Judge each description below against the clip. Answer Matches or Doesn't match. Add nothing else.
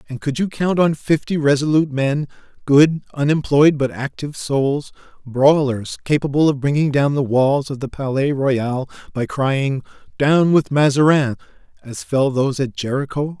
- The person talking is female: Doesn't match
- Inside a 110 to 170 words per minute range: Matches